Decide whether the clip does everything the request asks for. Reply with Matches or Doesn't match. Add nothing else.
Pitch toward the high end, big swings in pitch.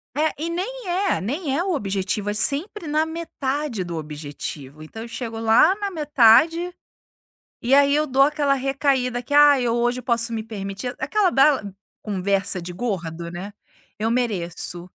Matches